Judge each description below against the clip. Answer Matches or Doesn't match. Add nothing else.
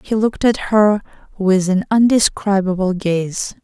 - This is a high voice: Matches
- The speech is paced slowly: Matches